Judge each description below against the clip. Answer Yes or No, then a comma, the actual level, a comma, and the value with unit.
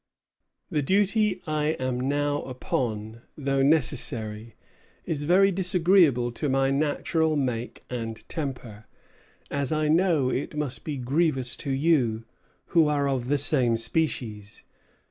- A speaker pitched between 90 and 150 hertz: Yes, medium, 140 Hz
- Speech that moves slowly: Yes, slow, 125 wpm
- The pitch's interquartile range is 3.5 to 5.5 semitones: Yes, average, 4.2 semitones